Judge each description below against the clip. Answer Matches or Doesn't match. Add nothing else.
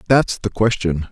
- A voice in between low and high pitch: Doesn't match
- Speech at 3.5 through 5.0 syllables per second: Matches